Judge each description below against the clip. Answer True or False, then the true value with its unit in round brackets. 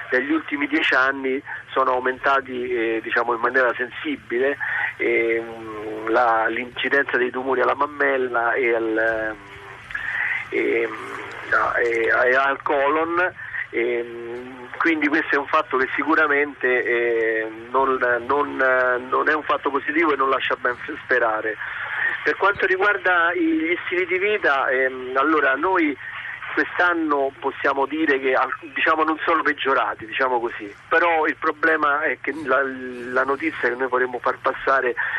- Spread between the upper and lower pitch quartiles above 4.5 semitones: True (5.2 semitones)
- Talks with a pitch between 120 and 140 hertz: True (130 Hz)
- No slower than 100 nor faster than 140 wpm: True (135 wpm)